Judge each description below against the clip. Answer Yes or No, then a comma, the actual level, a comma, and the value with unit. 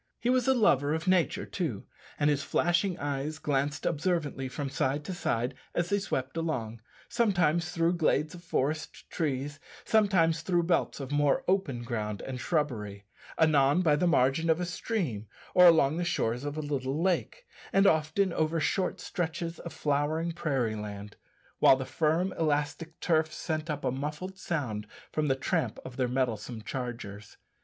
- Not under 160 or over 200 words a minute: Yes, average, 165 wpm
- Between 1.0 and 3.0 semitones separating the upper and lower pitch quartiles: No, average, 4.5 semitones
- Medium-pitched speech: Yes, medium, 150 Hz